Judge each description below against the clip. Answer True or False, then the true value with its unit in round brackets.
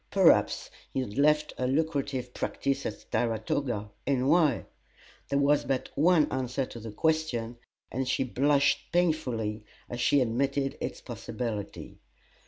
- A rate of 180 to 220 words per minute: False (135 wpm)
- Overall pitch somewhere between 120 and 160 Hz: True (135 Hz)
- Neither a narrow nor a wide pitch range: True (3.2 semitones)